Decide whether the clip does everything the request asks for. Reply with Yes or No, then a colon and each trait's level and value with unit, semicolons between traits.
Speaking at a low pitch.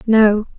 No: high, 215 Hz